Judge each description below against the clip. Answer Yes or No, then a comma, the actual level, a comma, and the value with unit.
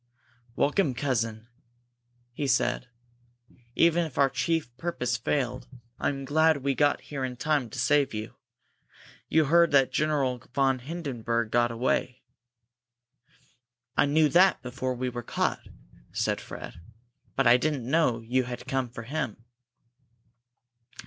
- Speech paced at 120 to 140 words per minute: Yes, slow, 135 wpm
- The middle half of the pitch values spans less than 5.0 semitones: Yes, average, 3.4 semitones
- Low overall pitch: Yes, low, 130 Hz